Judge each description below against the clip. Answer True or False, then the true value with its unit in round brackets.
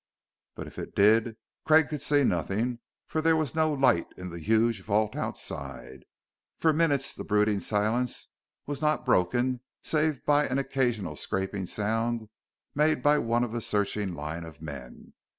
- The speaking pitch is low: True (115 Hz)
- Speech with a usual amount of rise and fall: False (6.3 semitones)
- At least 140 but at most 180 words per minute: True (160 wpm)